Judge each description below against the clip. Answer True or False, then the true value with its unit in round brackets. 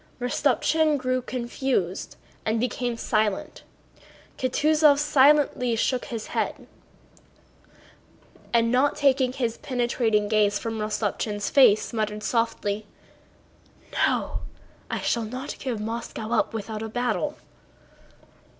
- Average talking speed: False (105 wpm)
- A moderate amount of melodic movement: True (3.2 semitones)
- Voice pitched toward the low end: False (235 Hz)